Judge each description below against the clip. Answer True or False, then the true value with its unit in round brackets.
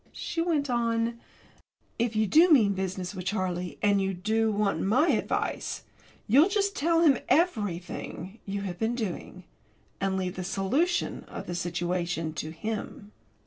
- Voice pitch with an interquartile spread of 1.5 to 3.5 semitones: False (4.8 semitones)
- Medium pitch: False (205 Hz)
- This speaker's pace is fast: False (150 wpm)